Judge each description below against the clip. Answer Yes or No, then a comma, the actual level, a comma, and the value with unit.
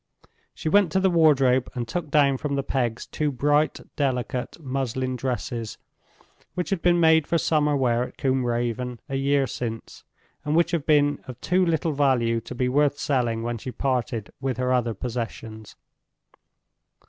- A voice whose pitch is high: No, low, 135 Hz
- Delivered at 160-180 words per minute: Yes, average, 170 wpm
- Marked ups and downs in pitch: No, average, 3.5 semitones